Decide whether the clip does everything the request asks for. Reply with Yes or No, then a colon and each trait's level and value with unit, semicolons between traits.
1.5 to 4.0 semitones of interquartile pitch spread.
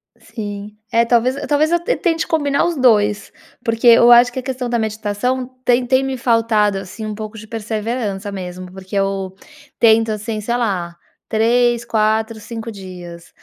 Yes: average, 2.9 semitones